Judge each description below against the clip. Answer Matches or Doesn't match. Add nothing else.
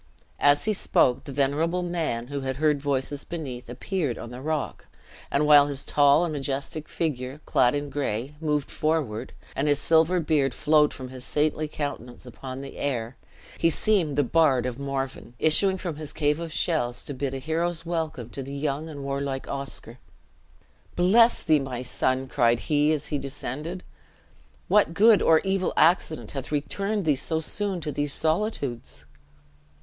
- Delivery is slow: Doesn't match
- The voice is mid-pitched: Matches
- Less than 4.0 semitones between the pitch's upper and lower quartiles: Matches